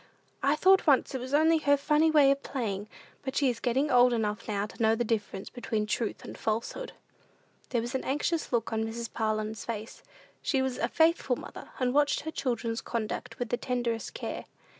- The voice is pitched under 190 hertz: No, high, 245 Hz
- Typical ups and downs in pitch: Yes, average, 3.9 semitones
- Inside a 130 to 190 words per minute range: No, average, 200 wpm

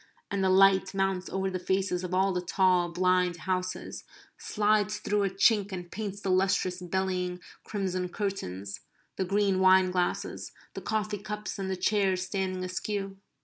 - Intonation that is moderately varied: No, narrow, 1.3 semitones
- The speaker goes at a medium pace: Yes, average, 160 wpm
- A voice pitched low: No, high, 190 Hz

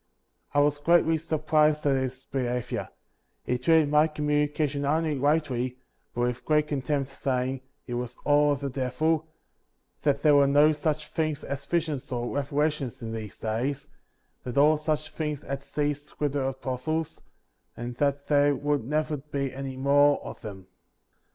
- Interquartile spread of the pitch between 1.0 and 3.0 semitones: Yes, narrow, 2.4 semitones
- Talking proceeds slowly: No, average, 165 wpm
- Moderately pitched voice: Yes, medium, 145 Hz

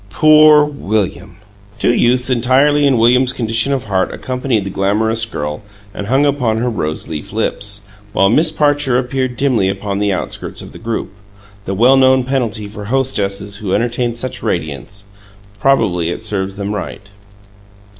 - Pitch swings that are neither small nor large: Yes, average, 4.5 semitones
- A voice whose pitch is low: Yes, low, 115 Hz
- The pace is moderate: Yes, average, 155 wpm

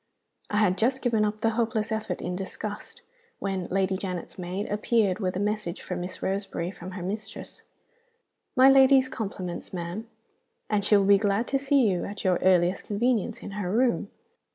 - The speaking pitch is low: No, high, 205 Hz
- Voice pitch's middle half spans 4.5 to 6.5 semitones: No, average, 3.3 semitones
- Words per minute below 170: No, average, 175 wpm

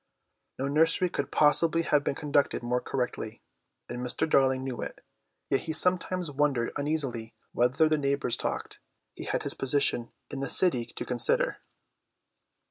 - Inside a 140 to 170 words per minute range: Yes, average, 150 wpm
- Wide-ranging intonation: No, average, 3.8 semitones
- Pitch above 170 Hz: No, medium, 140 Hz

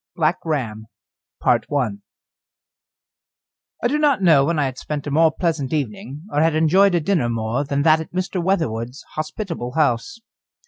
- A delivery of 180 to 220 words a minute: No, average, 150 wpm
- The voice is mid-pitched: Yes, medium, 155 Hz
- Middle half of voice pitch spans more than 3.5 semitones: Yes, average, 4.5 semitones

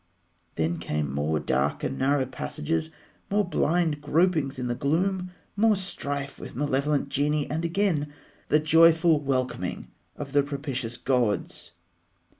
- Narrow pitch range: No, average, 3.8 semitones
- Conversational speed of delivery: No, slow, 130 wpm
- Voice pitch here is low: No, medium, 145 Hz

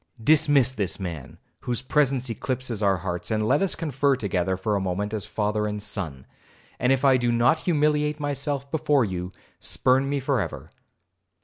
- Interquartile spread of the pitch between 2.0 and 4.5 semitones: No, wide, 5.6 semitones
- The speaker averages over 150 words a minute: Yes, average, 175 wpm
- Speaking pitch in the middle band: No, low, 125 Hz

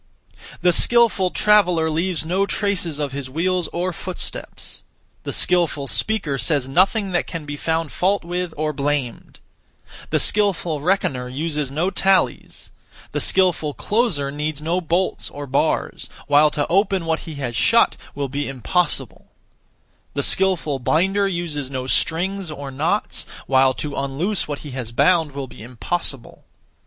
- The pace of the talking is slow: No, average, 145 wpm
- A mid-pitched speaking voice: Yes, medium, 160 Hz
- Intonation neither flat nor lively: Yes, average, 4.6 semitones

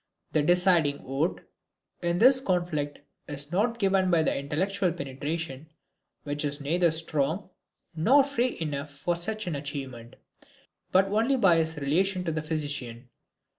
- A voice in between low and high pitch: Yes, medium, 165 Hz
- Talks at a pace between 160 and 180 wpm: No, average, 140 wpm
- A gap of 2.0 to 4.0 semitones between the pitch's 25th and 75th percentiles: No, average, 4.6 semitones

